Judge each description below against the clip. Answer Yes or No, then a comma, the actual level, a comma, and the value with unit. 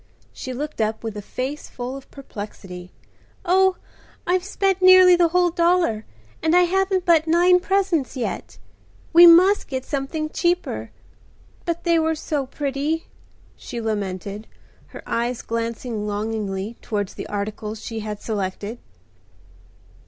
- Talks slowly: Yes, slow, 130 wpm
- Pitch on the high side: Yes, very high, 275 Hz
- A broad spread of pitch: Yes, wide, 8.1 semitones